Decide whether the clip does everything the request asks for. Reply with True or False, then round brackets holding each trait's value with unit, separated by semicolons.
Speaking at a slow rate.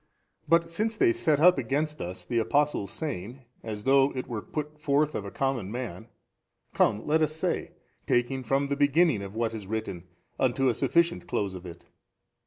False (190 wpm)